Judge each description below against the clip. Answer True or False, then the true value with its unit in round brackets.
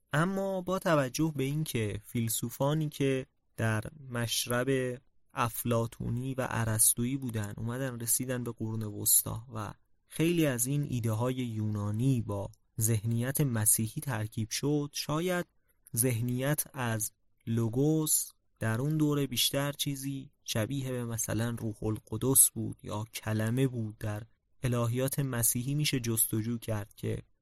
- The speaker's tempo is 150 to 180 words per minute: False (120 wpm)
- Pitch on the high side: False (120 Hz)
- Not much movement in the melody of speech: False (3.7 semitones)